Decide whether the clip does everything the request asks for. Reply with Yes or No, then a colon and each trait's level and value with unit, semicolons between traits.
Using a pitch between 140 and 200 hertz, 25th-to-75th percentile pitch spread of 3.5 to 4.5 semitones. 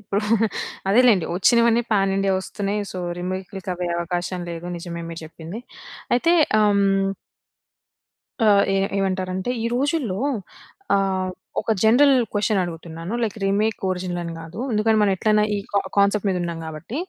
No: high, 195 Hz; average, 3.0 semitones